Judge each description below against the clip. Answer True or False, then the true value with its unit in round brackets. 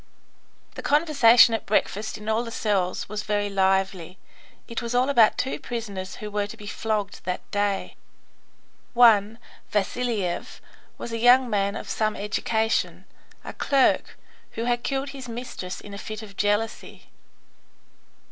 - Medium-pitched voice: False (215 Hz)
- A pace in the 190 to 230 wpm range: False (145 wpm)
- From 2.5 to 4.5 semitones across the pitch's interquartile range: True (2.9 semitones)